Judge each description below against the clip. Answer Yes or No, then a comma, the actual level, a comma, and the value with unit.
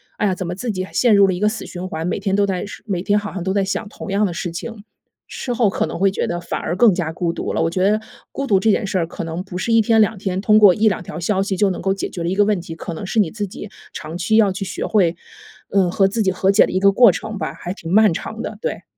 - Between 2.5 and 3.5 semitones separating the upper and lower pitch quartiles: Yes, average, 2.8 semitones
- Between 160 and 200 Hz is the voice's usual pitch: Yes, high, 195 Hz